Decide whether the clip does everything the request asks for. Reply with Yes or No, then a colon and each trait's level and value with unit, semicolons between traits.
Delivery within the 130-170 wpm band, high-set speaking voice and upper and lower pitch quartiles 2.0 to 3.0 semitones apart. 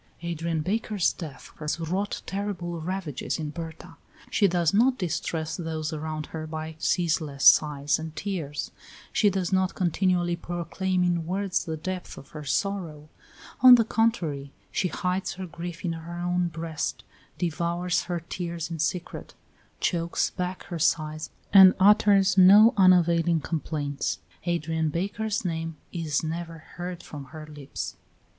No: average, 140 wpm; medium, 170 Hz; average, 2.7 semitones